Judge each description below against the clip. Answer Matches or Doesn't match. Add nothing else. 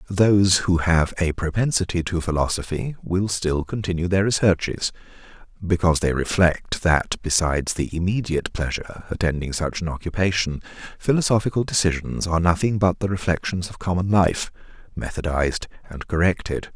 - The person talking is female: Doesn't match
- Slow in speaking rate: Matches